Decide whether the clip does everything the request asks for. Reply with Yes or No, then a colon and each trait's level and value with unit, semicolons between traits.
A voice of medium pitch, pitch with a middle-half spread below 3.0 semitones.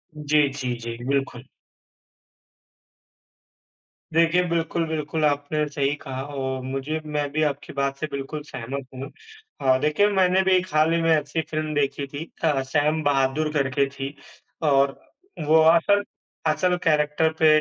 Yes: medium, 150 Hz; narrow, 2.4 semitones